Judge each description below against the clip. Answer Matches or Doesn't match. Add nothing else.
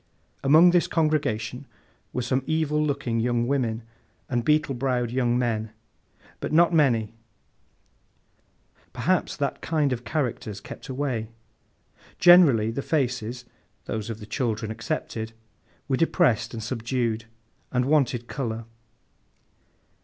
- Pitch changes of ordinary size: Matches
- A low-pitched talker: Matches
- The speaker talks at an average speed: Doesn't match